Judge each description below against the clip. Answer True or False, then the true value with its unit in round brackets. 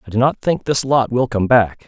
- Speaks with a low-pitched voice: True (120 Hz)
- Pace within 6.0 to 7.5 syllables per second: False (5.3 syllables/s)